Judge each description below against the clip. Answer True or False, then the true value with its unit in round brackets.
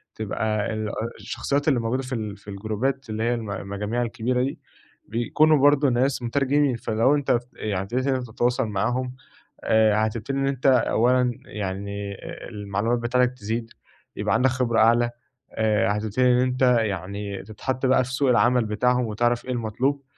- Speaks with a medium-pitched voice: False (120 Hz)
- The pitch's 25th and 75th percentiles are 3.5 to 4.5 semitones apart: False (3.1 semitones)